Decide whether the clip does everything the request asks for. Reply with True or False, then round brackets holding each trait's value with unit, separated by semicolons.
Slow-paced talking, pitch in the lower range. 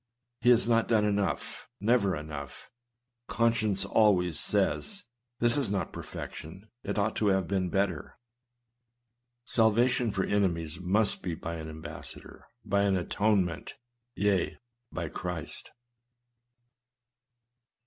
True (130 wpm; 100 Hz)